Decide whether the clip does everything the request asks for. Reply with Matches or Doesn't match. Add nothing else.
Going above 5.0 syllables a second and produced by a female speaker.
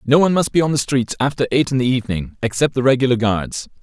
Doesn't match